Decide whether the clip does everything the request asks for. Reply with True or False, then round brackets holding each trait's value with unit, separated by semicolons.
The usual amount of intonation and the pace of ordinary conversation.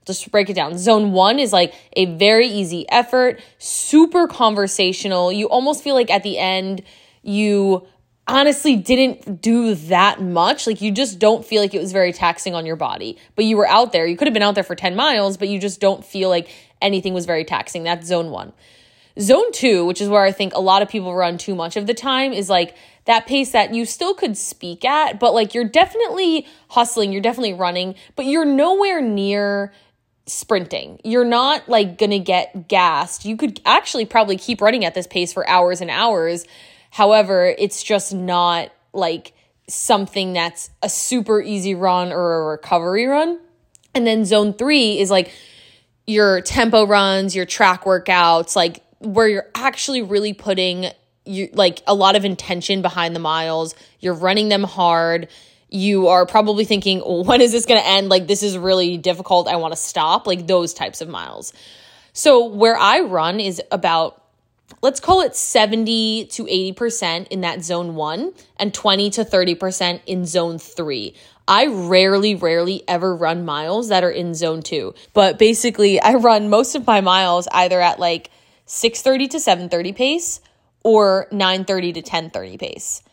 True (3.9 semitones; 180 wpm)